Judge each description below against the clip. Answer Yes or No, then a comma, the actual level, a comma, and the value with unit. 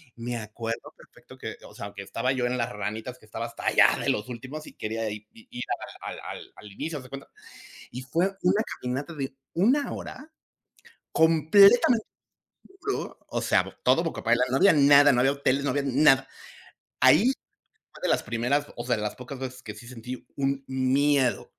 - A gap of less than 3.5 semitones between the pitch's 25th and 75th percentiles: No, average, 3.8 semitones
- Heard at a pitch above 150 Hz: No, low, 130 Hz